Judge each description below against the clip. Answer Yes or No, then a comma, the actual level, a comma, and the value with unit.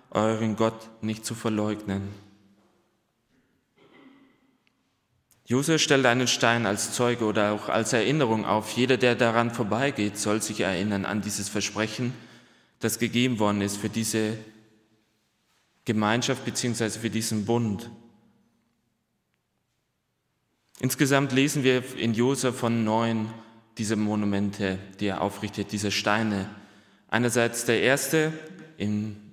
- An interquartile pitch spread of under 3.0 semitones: Yes, narrow, 2.6 semitones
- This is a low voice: Yes, low, 110 Hz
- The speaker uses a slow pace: Yes, slow, 115 wpm